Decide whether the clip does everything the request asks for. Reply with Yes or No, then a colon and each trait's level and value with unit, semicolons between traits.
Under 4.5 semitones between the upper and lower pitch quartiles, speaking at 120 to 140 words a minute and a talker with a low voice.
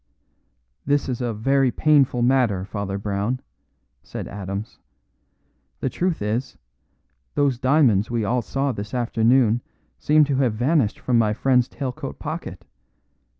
Yes: average, 4.1 semitones; slow, 135 wpm; low, 120 Hz